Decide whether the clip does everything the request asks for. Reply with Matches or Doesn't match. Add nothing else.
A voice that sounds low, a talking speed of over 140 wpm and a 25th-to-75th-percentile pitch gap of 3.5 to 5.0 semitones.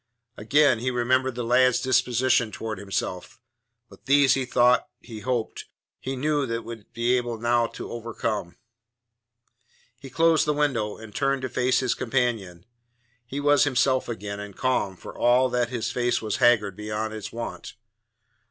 Doesn't match